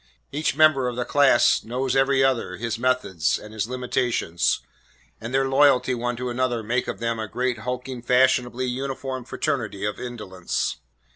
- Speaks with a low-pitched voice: Yes, low, 125 Hz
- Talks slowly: No, average, 160 wpm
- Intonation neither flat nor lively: No, narrow, 2.1 semitones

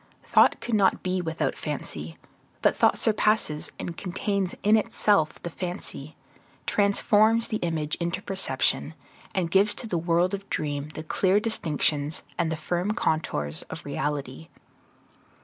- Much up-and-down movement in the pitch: No, average, 4.6 semitones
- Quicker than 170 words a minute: No, average, 140 wpm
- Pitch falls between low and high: Yes, medium, 175 Hz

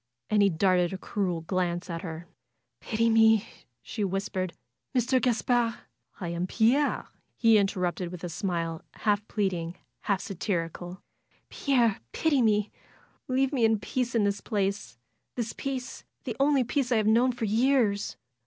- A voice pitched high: Yes, high, 205 Hz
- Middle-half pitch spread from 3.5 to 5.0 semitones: Yes, average, 4.5 semitones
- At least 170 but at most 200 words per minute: No, average, 155 wpm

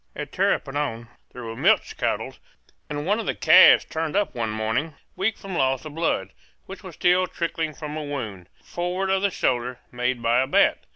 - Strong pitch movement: Yes, wide, 6.4 semitones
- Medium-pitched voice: Yes, medium, 145 Hz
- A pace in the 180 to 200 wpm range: Yes, average, 190 wpm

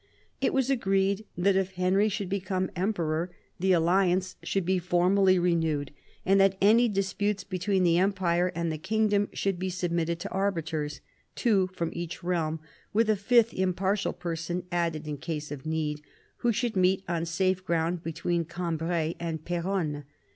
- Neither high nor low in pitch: Yes, medium, 180 Hz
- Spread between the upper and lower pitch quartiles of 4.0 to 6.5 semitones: No, narrow, 2.6 semitones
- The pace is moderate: Yes, average, 170 wpm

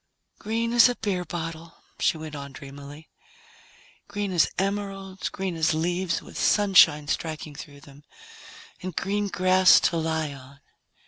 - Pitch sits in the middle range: Yes, medium, 170 Hz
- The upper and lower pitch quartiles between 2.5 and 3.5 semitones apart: No, average, 4.4 semitones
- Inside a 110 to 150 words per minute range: Yes, average, 140 wpm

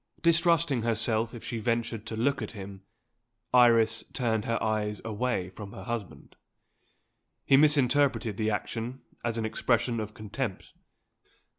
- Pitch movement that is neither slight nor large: No, narrow, 2.3 semitones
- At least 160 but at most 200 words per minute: No, slow, 135 wpm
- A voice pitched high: No, low, 115 Hz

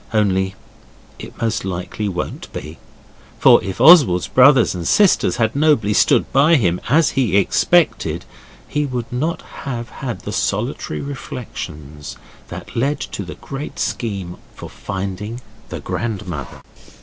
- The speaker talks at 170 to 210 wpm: No, slow, 135 wpm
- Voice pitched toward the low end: Yes, low, 110 Hz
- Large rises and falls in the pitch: Yes, wide, 6.7 semitones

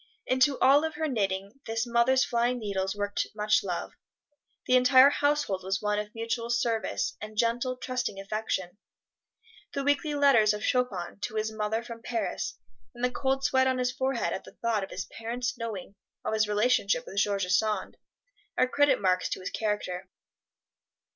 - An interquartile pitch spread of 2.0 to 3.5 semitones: No, average, 3.9 semitones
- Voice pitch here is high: Yes, high, 225 Hz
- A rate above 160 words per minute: Yes, average, 170 wpm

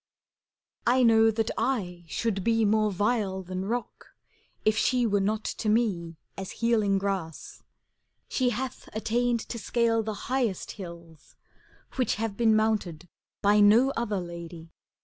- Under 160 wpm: Yes, average, 140 wpm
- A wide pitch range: No, average, 3.5 semitones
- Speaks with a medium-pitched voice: No, high, 215 Hz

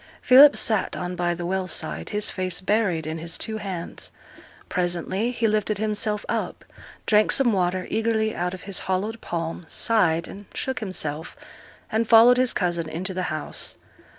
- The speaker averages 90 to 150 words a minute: No, average, 165 wpm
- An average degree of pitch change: Yes, average, 3.8 semitones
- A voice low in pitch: No, high, 190 Hz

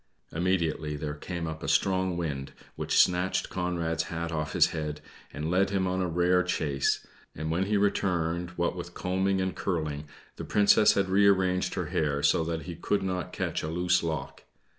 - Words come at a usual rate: Yes, average, 175 wpm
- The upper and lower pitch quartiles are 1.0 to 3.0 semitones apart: Yes, narrow, 2.6 semitones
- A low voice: Yes, very low, 85 Hz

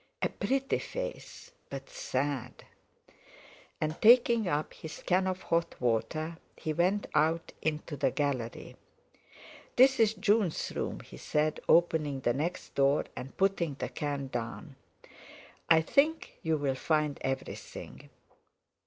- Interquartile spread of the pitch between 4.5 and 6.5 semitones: Yes, average, 5.3 semitones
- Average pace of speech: No, slow, 125 wpm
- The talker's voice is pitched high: No, medium, 160 Hz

